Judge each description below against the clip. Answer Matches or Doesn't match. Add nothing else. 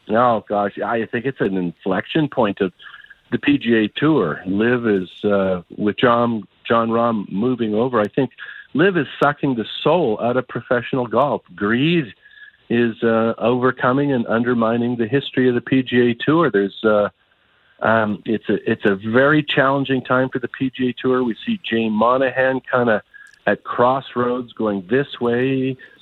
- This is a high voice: Doesn't match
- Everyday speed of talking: Matches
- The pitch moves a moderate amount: Matches